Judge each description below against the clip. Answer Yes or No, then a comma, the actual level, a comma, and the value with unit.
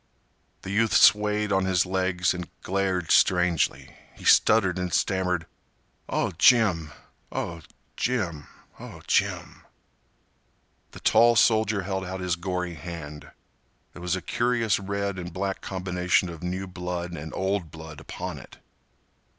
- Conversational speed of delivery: No, slow, 125 wpm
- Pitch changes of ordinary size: No, narrow, 2.2 semitones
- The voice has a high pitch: No, very low, 90 Hz